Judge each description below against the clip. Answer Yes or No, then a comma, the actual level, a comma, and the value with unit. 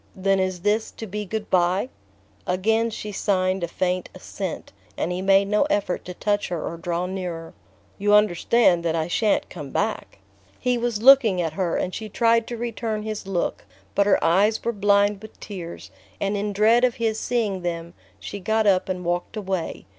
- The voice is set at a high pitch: Yes, high, 200 Hz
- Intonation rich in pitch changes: No, average, 3.3 semitones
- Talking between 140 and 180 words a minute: No, average, 190 wpm